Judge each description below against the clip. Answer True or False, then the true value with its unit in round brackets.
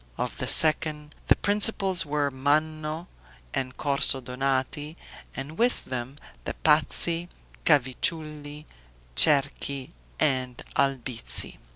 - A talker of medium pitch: True (145 Hz)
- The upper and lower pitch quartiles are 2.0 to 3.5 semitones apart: True (2.8 semitones)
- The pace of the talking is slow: True (95 wpm)